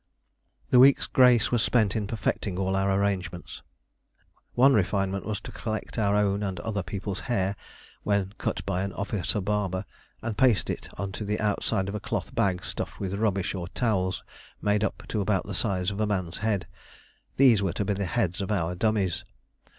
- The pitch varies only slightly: Yes, narrow, 2.1 semitones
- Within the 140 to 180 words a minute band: No, average, 190 wpm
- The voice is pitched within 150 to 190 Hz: No, low, 100 Hz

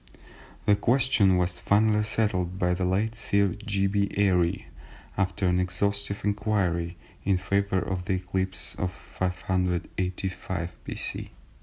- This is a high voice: No, very low, 95 Hz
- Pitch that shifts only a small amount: Yes, narrow, 1.9 semitones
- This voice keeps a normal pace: No, slow, 125 wpm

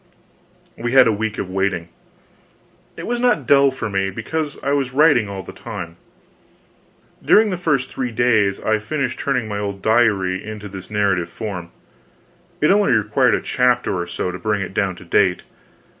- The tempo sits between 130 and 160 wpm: No, average, 175 wpm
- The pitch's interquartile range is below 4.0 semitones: No, wide, 5.4 semitones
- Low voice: Yes, low, 110 Hz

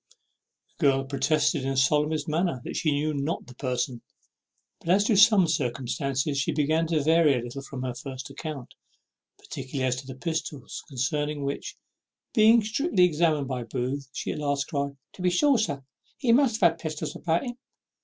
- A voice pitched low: No, medium, 145 Hz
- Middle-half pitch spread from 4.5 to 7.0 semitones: No, average, 3.7 semitones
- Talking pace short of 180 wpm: No, average, 185 wpm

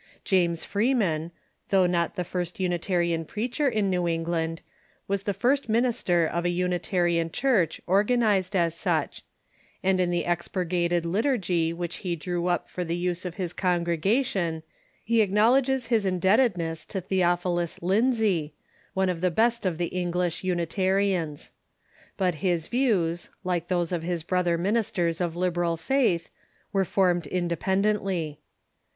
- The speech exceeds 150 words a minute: No, average, 145 wpm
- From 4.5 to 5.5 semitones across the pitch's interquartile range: No, narrow, 2.6 semitones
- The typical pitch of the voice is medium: Yes, medium, 180 Hz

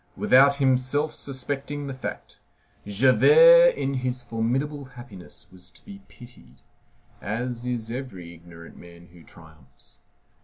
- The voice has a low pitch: Yes, low, 125 Hz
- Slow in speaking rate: Yes, slow, 120 wpm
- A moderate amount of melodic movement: No, wide, 6.6 semitones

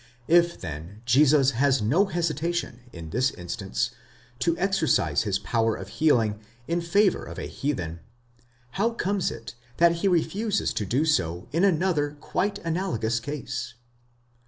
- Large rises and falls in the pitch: Yes, wide, 7.3 semitones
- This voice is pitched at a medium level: Yes, medium, 145 Hz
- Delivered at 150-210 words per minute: No, average, 140 wpm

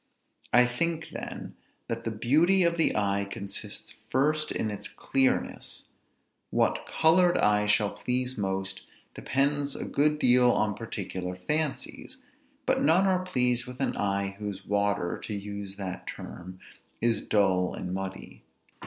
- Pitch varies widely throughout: Yes, wide, 6.2 semitones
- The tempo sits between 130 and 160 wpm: Yes, average, 140 wpm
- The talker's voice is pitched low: Yes, low, 115 Hz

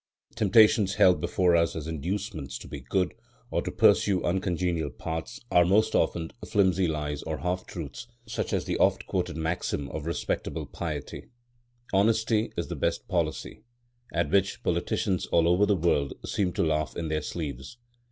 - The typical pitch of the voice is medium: No, very low, 85 Hz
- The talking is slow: No, average, 160 wpm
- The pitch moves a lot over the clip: No, average, 3.7 semitones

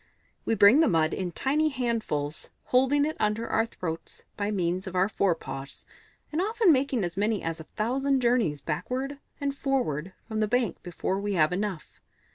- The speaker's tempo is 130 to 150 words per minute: No, average, 175 wpm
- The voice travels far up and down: Yes, wide, 7.3 semitones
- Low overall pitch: No, high, 210 Hz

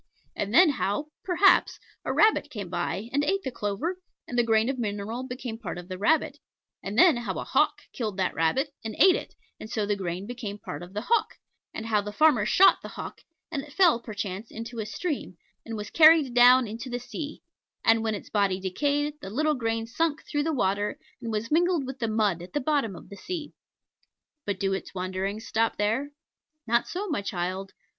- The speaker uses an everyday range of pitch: No, wide, 6.1 semitones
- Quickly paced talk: Yes, fast, 210 wpm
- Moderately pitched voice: No, high, 230 Hz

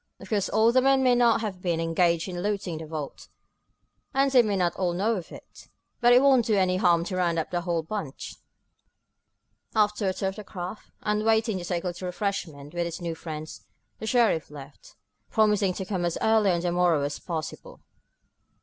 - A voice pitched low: No, medium, 185 Hz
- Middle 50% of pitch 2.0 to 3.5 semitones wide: No, average, 4.1 semitones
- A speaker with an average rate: No, fast, 210 wpm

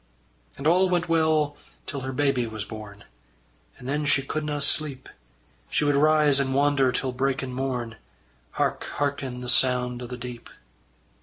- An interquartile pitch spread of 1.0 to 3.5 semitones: Yes, average, 2.8 semitones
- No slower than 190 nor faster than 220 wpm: No, average, 155 wpm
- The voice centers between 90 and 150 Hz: Yes, low, 135 Hz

